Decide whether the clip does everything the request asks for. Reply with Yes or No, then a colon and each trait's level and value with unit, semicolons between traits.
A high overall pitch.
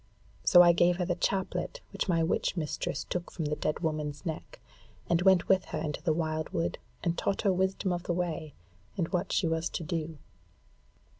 No: medium, 170 Hz